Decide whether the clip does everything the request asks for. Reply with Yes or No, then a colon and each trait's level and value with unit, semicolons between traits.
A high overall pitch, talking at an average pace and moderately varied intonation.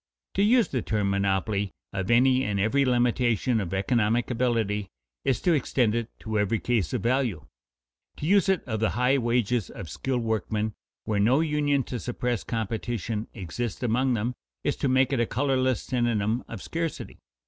No: low, 120 Hz; average, 170 wpm; average, 3.4 semitones